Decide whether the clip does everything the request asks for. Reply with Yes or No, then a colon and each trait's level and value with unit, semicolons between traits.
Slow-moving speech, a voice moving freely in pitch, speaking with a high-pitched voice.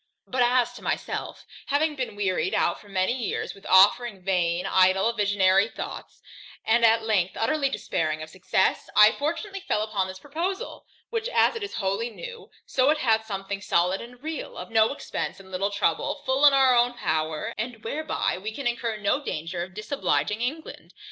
No: average, 180 wpm; wide, 5.9 semitones; high, 220 Hz